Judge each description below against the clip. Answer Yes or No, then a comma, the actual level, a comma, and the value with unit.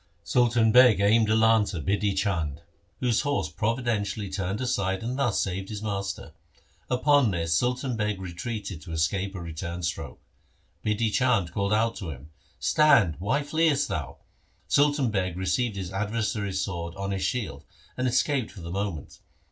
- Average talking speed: Yes, average, 165 wpm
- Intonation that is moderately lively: Yes, average, 4.5 semitones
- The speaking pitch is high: No, low, 100 Hz